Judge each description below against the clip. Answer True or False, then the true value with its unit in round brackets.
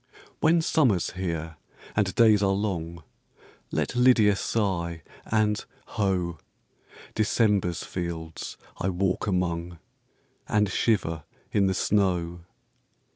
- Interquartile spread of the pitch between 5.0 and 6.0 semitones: False (3.6 semitones)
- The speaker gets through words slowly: True (100 wpm)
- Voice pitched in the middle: False (95 Hz)